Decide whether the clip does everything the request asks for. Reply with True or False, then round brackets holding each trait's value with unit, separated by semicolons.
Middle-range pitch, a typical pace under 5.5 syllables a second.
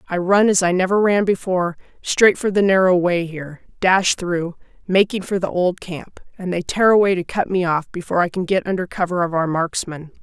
True (180 Hz; 5.3 syllables/s)